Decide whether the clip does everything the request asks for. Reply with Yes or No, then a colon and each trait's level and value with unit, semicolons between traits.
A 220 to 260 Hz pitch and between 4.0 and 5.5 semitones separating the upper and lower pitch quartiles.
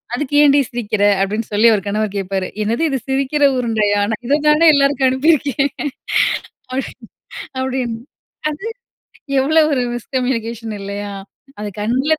Yes: very high, 250 Hz; average, 4.5 semitones